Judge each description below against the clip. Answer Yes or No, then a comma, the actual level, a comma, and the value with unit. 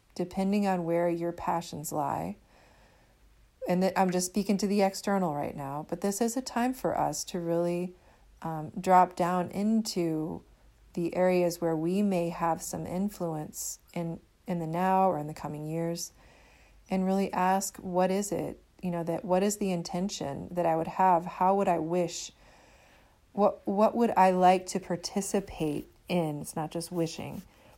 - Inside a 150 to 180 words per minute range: Yes, average, 170 wpm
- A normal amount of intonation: No, narrow, 2.3 semitones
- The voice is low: No, medium, 180 Hz